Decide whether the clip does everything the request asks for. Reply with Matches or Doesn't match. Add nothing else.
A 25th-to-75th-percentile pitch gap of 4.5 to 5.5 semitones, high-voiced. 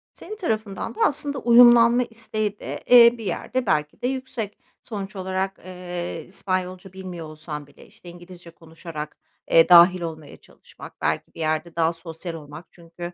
Doesn't match